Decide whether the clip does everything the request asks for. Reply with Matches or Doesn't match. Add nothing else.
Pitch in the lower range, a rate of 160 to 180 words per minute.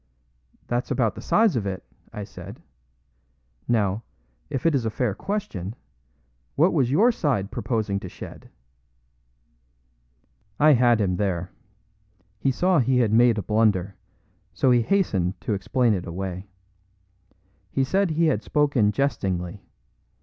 Doesn't match